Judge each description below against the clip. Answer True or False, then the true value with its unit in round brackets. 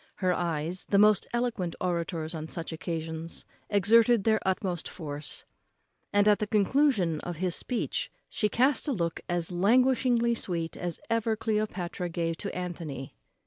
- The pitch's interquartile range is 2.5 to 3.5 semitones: False (4.9 semitones)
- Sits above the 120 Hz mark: True (185 Hz)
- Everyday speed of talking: True (145 wpm)